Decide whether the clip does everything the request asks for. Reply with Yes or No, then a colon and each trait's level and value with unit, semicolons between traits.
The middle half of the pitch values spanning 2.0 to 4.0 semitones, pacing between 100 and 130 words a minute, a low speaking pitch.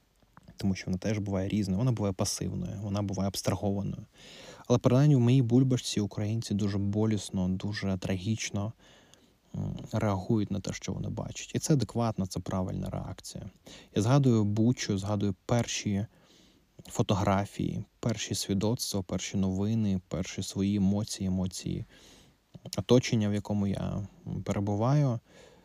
Yes: average, 2.8 semitones; average, 125 wpm; low, 105 Hz